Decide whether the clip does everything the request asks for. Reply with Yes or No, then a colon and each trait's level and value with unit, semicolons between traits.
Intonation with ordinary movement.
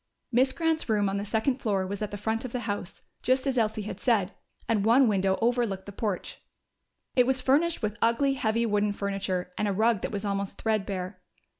Yes: average, 3.4 semitones